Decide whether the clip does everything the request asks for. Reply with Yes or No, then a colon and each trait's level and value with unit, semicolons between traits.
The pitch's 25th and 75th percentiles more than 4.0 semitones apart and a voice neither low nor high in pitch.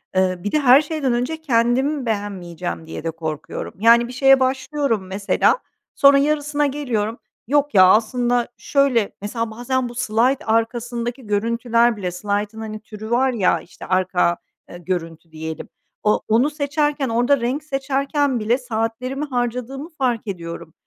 No: average, 4.6 semitones; high, 235 Hz